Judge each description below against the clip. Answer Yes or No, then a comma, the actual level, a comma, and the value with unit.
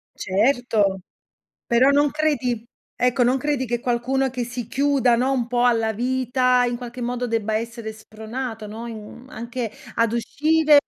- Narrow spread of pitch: Yes, narrow, 2.2 semitones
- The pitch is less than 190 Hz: No, high, 245 Hz